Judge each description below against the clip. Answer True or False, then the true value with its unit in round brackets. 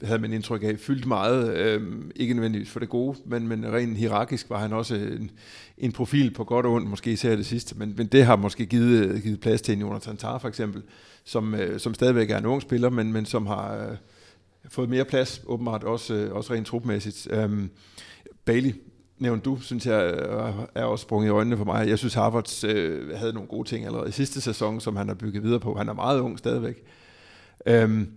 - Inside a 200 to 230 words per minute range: True (210 wpm)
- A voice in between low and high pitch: False (115 Hz)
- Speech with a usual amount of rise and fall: False (2.1 semitones)